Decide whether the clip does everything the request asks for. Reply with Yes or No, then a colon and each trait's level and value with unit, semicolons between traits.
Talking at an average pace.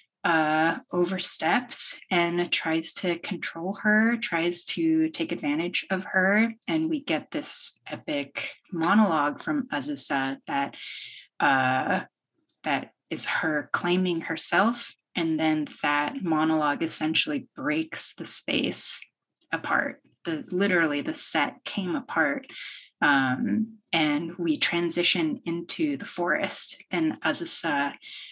No: slow, 110 wpm